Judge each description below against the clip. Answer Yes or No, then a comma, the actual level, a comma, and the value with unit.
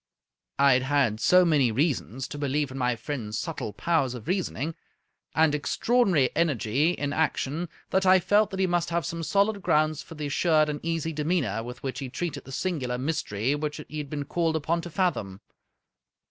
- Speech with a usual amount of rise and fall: Yes, average, 4.2 semitones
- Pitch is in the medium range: Yes, medium, 150 Hz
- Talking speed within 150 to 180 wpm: No, average, 190 wpm